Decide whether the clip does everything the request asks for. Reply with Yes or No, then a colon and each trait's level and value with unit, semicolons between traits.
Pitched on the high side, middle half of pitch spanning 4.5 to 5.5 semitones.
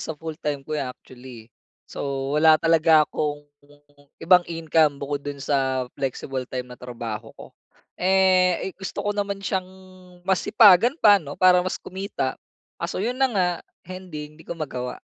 No: medium, 155 Hz; average, 5.1 semitones